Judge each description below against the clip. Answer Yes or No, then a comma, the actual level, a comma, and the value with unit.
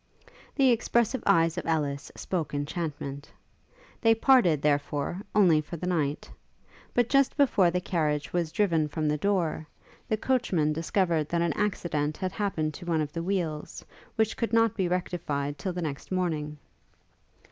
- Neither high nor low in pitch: Yes, medium, 170 Hz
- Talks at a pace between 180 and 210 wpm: No, average, 160 wpm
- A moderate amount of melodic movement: Yes, average, 4.6 semitones